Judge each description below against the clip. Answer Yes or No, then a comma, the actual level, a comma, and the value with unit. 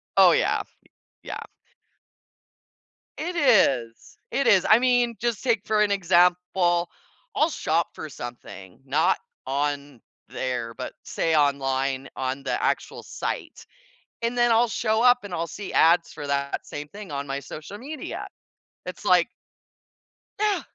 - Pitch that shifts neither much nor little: No, wide, 8.6 semitones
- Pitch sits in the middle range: Yes, medium, 175 Hz